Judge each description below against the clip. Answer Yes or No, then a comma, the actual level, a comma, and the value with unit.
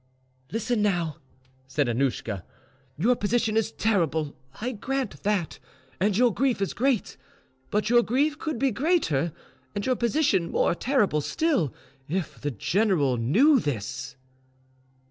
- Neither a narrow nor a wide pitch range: No, wide, 8.3 semitones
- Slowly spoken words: Yes, slow, 130 wpm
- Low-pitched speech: No, high, 210 Hz